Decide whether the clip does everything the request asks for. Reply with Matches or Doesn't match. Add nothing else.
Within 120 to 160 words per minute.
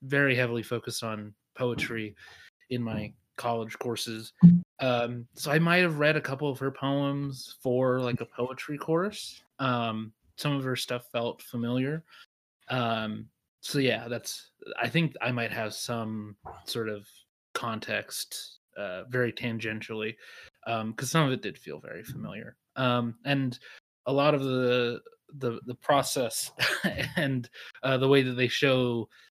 Matches